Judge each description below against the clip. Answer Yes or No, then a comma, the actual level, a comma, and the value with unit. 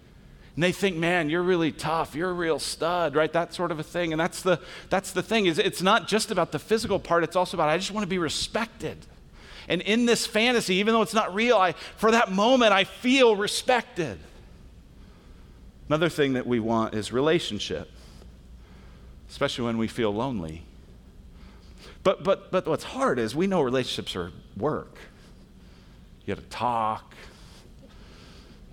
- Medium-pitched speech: Yes, medium, 160 Hz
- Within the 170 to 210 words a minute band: Yes, average, 175 wpm